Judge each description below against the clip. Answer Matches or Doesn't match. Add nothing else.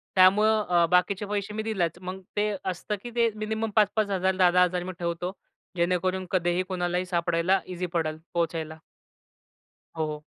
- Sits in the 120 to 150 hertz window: Doesn't match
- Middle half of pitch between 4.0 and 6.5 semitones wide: Doesn't match